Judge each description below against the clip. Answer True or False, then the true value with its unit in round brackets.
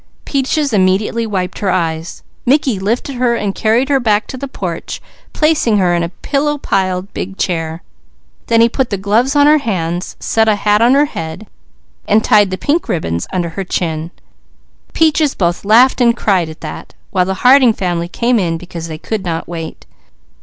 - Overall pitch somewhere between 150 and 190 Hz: False (205 Hz)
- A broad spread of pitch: True (5.9 semitones)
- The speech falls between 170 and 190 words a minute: True (175 wpm)